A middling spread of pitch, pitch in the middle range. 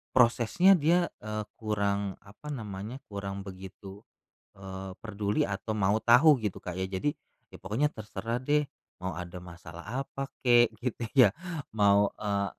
No: average, 3.7 semitones; low, 105 Hz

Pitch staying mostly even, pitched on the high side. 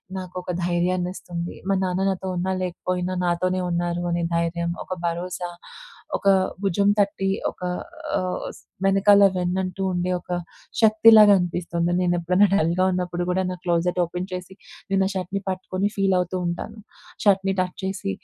No: narrow, 1.6 semitones; medium, 180 Hz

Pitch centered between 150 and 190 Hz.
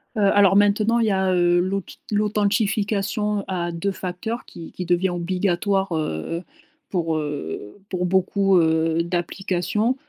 Yes: medium, 185 Hz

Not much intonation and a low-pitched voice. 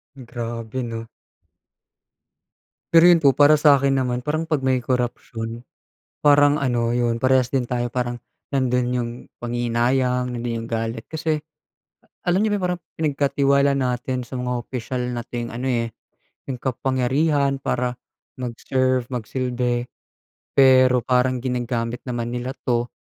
Yes: narrow, 2.2 semitones; low, 125 Hz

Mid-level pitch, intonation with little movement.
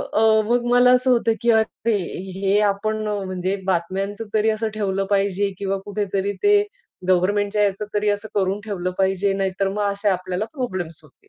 No: high, 200 Hz; narrow, 2.1 semitones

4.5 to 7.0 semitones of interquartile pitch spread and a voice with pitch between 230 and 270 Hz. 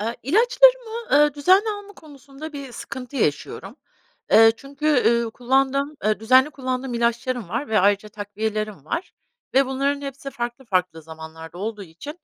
Yes: average, 5.1 semitones; very high, 255 Hz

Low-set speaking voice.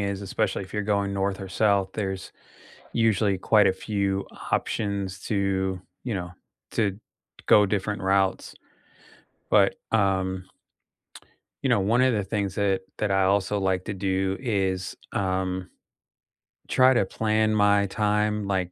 Yes: low, 100 Hz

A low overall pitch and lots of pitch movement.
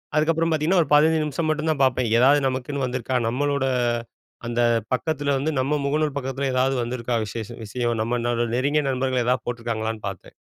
No: low, 130 Hz; average, 3.5 semitones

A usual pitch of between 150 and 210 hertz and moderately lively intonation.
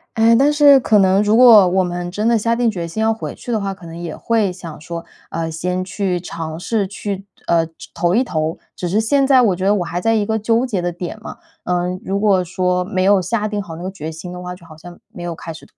Yes: medium, 185 Hz; average, 3.9 semitones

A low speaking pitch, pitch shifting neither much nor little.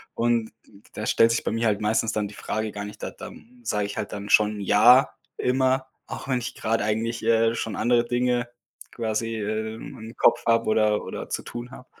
No: low, 115 Hz; narrow, 1.9 semitones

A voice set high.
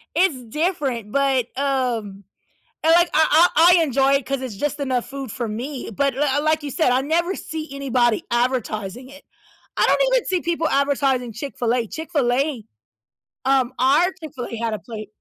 Yes: very high, 270 Hz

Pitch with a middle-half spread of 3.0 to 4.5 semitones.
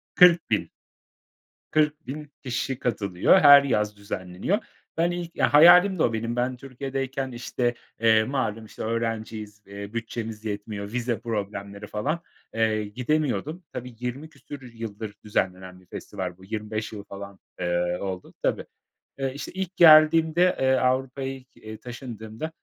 No: average, 5.0 semitones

